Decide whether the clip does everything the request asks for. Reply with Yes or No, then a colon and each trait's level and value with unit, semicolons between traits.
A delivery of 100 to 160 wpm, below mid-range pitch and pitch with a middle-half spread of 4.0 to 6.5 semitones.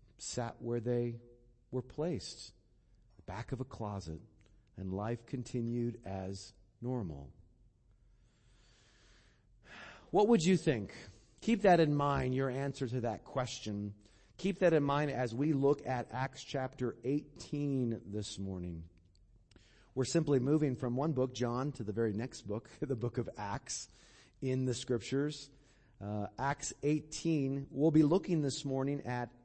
Yes: average, 140 wpm; low, 120 Hz; average, 4.3 semitones